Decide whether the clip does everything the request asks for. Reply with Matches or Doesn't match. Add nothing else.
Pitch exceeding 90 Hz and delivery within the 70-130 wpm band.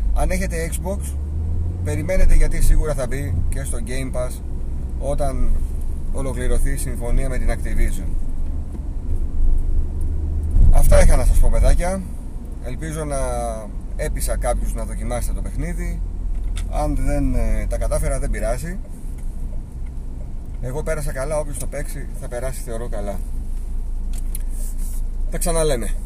Doesn't match